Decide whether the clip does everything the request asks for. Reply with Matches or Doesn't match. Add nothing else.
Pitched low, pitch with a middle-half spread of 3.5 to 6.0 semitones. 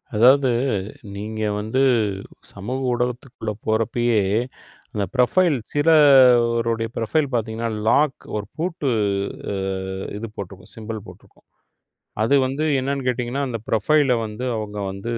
Matches